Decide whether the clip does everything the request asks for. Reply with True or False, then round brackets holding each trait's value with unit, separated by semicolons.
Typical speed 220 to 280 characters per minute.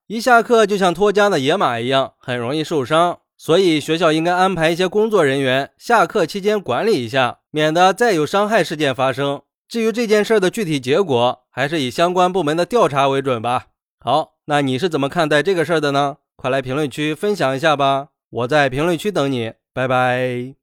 False (305 characters per minute)